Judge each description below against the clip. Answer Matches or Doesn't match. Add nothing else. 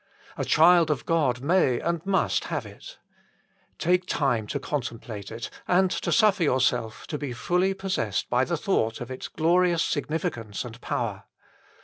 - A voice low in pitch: Doesn't match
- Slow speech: Doesn't match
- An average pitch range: Doesn't match